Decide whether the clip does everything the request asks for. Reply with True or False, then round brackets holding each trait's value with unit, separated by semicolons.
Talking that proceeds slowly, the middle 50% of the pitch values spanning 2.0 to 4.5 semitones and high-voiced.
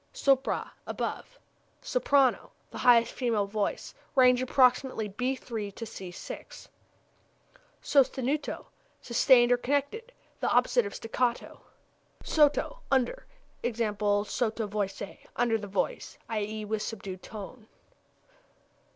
True (100 wpm; 3.9 semitones; 240 Hz)